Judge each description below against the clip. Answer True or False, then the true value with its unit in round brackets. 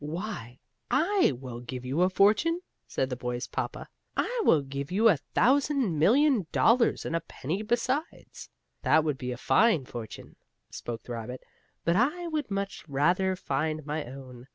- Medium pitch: True (165 Hz)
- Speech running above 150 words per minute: True (165 wpm)